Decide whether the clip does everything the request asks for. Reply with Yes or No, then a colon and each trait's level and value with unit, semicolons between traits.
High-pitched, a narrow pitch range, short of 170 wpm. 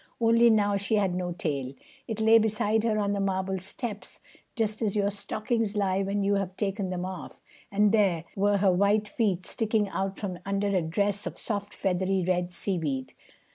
No: high, 200 Hz; narrow, 2.1 semitones; average, 185 wpm